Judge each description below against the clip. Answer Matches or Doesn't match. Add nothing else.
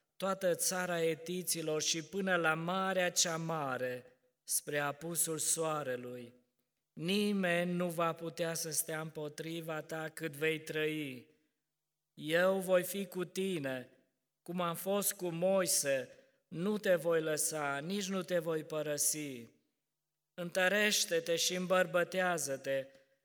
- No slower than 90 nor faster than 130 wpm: Matches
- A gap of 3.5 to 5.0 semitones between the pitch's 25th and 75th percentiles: Doesn't match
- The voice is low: Doesn't match